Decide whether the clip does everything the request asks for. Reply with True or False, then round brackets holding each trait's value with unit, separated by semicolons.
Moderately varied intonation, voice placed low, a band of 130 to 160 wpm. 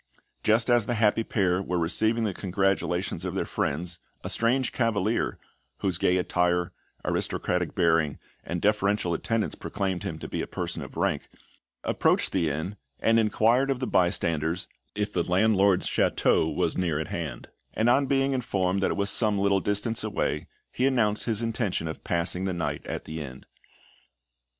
False (4.2 semitones; 95 Hz; 170 wpm)